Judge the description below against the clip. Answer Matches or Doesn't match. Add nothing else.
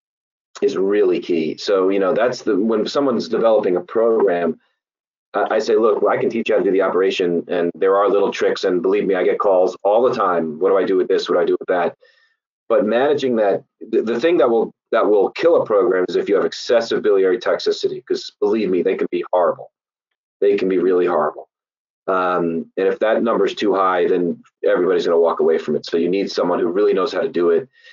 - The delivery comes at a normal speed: Doesn't match